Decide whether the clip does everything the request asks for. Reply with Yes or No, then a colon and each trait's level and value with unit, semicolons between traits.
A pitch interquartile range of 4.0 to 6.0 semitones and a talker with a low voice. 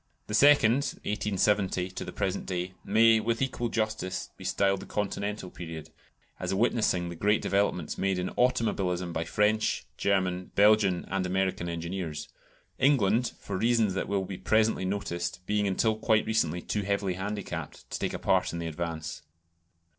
No: average, 3.0 semitones; low, 100 Hz